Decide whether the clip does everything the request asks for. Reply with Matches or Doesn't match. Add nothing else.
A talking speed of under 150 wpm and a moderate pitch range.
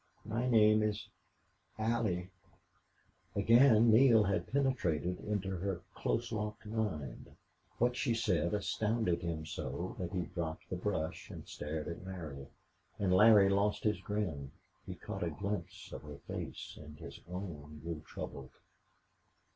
Matches